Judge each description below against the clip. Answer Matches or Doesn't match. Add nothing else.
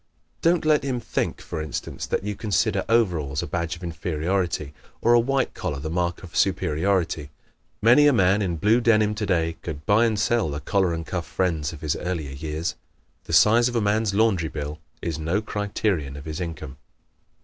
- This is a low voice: Matches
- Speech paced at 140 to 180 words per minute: Doesn't match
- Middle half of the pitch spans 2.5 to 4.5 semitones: Doesn't match